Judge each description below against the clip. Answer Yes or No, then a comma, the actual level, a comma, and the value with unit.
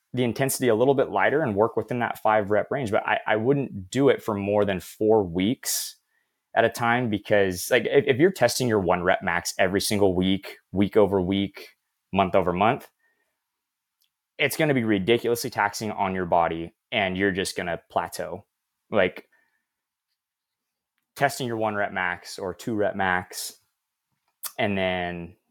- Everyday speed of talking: Yes, average, 170 wpm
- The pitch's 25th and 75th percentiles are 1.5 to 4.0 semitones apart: Yes, average, 3.5 semitones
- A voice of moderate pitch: No, low, 105 Hz